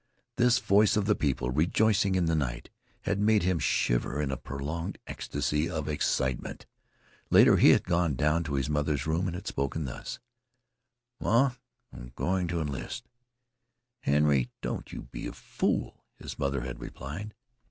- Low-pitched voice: Yes, very low, 80 Hz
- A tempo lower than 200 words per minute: Yes, average, 160 wpm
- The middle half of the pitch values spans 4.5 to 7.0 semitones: Yes, wide, 5.5 semitones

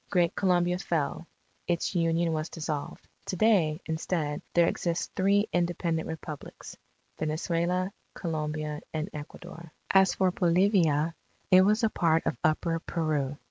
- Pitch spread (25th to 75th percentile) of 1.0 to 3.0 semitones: Yes, average, 2.7 semitones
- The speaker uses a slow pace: Yes, slow, 130 wpm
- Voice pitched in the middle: Yes, medium, 170 Hz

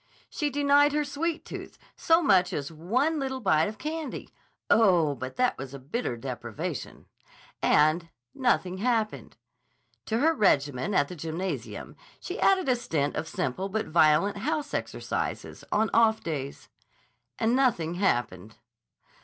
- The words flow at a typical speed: No, slow, 130 wpm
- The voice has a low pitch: No, high, 195 Hz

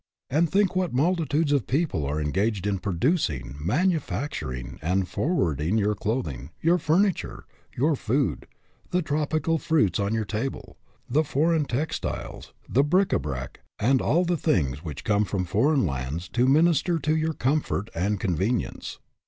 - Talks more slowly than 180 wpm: Yes, average, 155 wpm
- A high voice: No, low, 125 Hz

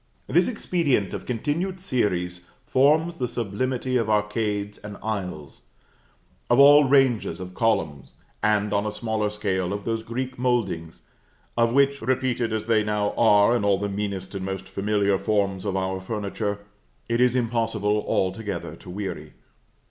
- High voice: No, low, 105 Hz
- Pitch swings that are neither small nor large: Yes, average, 3.8 semitones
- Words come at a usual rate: Yes, average, 150 wpm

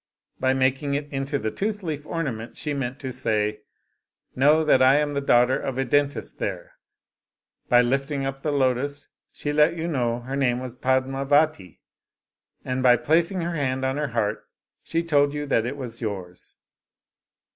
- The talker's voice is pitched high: No, low, 135 Hz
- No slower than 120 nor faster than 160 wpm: No, average, 175 wpm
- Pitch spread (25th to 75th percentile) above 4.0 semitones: No, average, 2.9 semitones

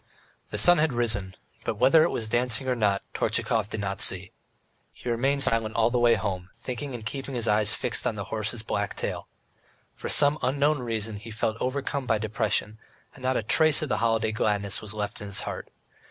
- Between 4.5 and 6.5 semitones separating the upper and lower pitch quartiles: No, average, 3.4 semitones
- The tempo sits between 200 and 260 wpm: Yes, fast, 205 wpm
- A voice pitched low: Yes, low, 115 Hz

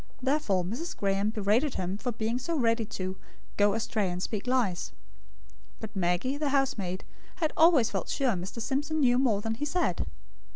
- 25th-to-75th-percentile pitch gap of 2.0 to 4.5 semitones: No, wide, 5.5 semitones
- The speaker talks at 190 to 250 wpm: No, average, 170 wpm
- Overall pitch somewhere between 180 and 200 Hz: No, high, 225 Hz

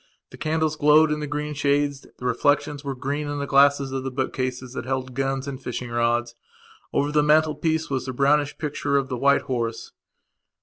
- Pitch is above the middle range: No, medium, 140 Hz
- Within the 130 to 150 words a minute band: No, average, 200 wpm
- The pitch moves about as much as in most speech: No, narrow, 2.3 semitones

